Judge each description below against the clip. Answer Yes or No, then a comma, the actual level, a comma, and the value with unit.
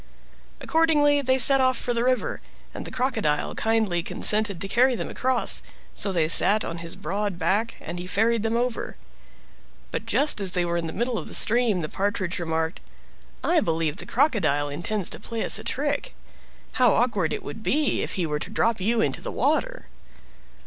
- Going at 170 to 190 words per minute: Yes, average, 185 wpm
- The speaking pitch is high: Yes, high, 220 Hz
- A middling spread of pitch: No, wide, 6.4 semitones